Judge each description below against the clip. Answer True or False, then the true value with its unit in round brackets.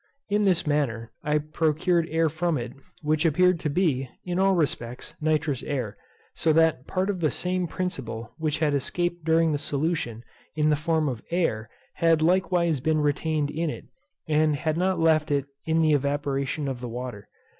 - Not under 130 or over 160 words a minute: False (175 wpm)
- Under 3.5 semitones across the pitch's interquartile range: True (3.0 semitones)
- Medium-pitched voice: True (155 Hz)